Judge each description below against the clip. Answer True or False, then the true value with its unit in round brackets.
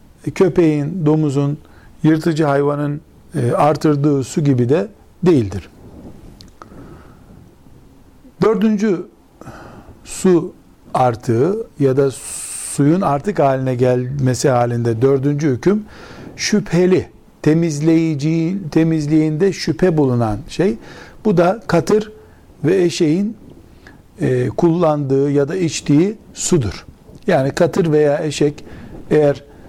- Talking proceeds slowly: True (85 wpm)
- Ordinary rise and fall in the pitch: True (4.0 semitones)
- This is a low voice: False (150 Hz)